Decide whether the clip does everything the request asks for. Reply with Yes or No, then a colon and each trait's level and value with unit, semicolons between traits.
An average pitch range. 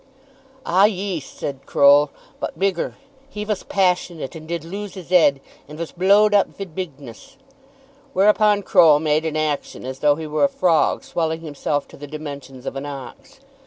Yes: average, 4.7 semitones